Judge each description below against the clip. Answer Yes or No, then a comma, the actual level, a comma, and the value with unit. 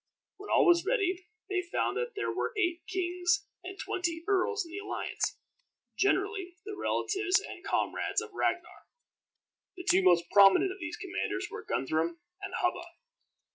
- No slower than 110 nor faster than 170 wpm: Yes, average, 155 wpm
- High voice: Yes, very high, 370 Hz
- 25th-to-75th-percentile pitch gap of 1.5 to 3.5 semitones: Yes, average, 2.7 semitones